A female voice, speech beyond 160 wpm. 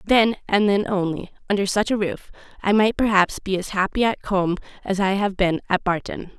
Yes: female; fast, 205 wpm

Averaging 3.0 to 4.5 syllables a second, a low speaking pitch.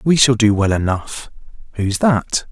Yes: 4.1 syllables/s; low, 115 Hz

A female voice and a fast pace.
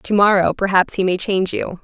Yes: female; fast, 230 wpm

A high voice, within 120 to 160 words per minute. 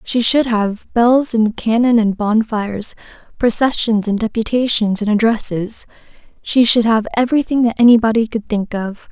Yes: high, 225 Hz; average, 140 wpm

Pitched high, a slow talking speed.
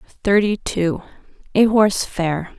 Yes: high, 195 Hz; slow, 115 wpm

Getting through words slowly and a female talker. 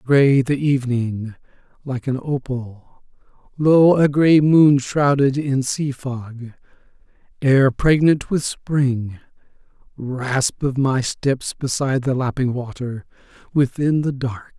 No: slow, 120 wpm; male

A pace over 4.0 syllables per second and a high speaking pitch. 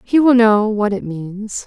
No: 3.8 syllables/s; high, 215 Hz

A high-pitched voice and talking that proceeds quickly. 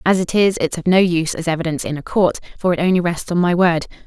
No: medium, 170 Hz; fast, 280 wpm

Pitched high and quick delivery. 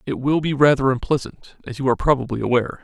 No: low, 130 Hz; fast, 210 wpm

